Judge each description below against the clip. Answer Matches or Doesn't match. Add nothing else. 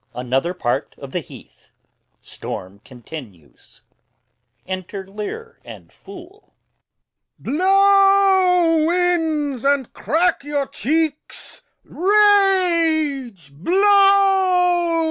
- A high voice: Matches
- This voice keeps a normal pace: Doesn't match